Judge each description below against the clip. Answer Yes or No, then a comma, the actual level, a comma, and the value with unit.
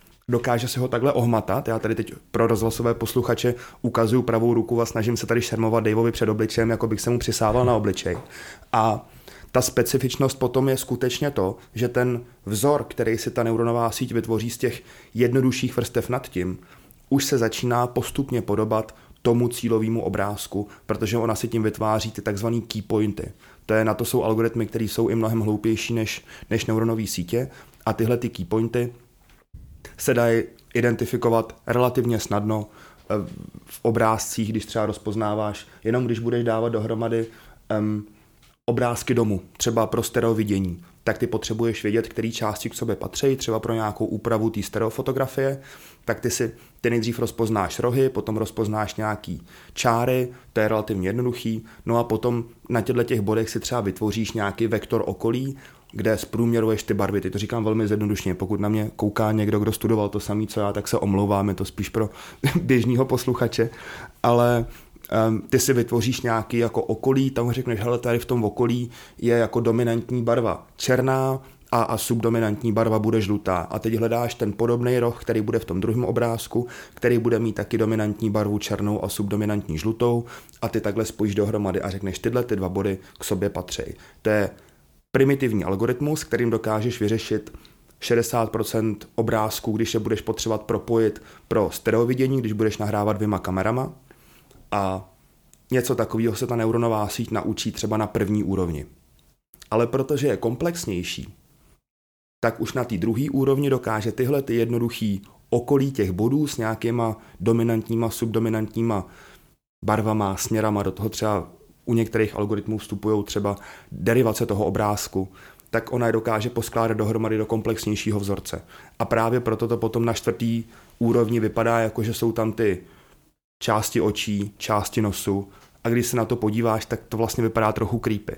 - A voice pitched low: Yes, low, 115 Hz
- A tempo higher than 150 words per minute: Yes, average, 160 wpm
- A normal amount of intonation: No, narrow, 1.9 semitones